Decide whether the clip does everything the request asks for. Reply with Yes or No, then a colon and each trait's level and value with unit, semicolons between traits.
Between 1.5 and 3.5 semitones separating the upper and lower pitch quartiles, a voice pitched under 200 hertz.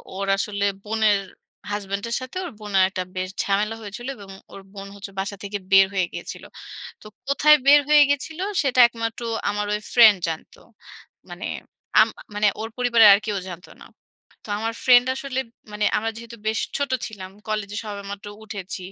No: average, 2.9 semitones; high, 210 Hz